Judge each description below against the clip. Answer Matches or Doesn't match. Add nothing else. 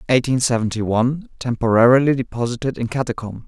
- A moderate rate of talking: Doesn't match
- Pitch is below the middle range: Matches